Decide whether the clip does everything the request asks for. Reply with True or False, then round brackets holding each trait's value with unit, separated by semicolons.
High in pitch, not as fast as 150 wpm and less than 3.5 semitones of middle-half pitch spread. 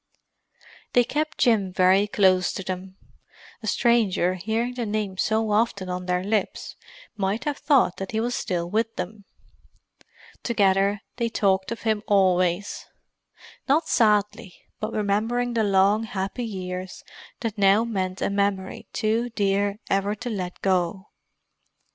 True (205 Hz; 140 wpm; 2.9 semitones)